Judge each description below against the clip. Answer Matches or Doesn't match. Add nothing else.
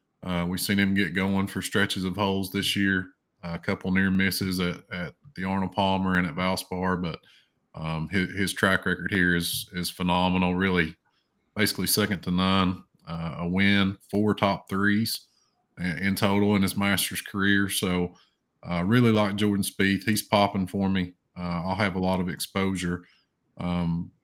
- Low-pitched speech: Matches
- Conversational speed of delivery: Matches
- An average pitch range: Doesn't match